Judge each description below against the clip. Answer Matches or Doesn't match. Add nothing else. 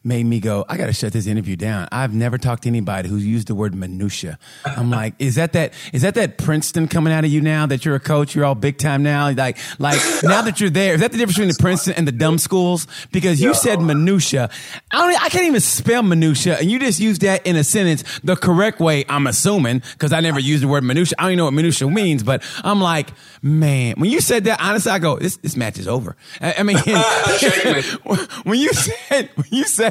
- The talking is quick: Matches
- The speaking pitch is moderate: Matches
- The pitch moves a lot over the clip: Matches